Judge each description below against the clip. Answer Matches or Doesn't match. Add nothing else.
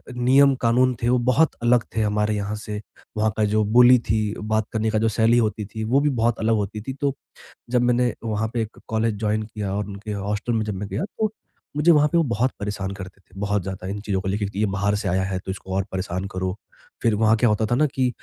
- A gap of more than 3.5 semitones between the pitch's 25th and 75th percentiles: Doesn't match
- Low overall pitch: Matches